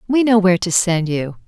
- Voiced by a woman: Yes, female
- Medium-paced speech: No, fast, 245 wpm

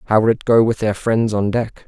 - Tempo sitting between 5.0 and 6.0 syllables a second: Yes, 5.4 syllables/s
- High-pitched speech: No, low, 110 Hz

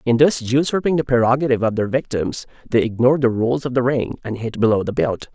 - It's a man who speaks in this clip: Yes, male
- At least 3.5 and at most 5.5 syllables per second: No, 6.0 syllables/s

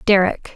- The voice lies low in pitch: No, high, 195 Hz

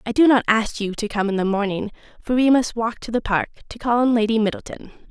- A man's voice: No, female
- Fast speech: Yes, fast, 260 wpm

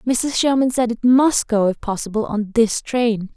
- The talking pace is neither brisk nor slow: Yes, average, 195 wpm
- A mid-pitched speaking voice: No, high, 230 Hz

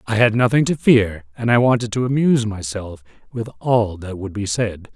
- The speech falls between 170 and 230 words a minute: Yes, fast, 205 wpm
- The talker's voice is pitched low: Yes, low, 110 Hz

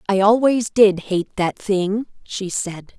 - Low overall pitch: No, high, 200 Hz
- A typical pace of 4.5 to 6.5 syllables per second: No, 3.5 syllables/s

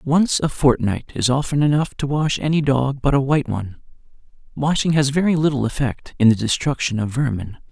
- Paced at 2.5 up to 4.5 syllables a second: No, 5.5 syllables/s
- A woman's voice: No, male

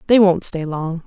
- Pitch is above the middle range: No, medium, 175 Hz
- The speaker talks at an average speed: No, fast, 225 wpm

